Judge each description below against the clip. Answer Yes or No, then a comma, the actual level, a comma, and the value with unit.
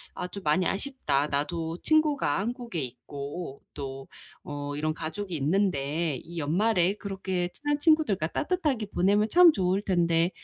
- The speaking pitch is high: No, medium, 180 Hz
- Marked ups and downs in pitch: Yes, wide, 5.9 semitones